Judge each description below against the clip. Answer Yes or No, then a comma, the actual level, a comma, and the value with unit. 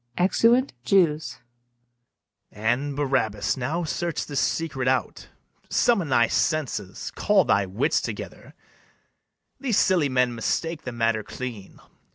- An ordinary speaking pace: No, slow, 115 wpm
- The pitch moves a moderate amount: No, wide, 6.1 semitones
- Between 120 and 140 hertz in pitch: Yes, low, 135 Hz